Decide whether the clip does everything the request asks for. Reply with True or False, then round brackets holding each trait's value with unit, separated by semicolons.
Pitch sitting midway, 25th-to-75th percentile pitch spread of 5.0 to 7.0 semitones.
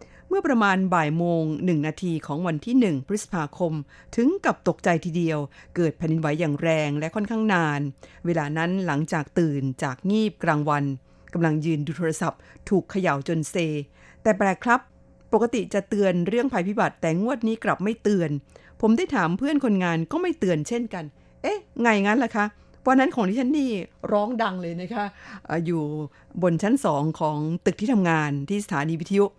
True (180 Hz; 5.3 semitones)